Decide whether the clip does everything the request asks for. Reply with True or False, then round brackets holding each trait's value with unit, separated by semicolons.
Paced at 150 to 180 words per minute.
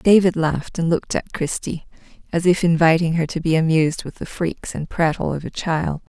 False (205 wpm)